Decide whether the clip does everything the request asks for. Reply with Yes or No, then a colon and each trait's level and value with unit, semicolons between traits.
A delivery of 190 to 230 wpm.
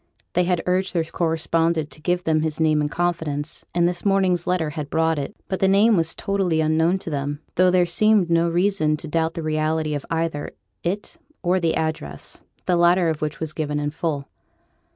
Yes: average, 200 wpm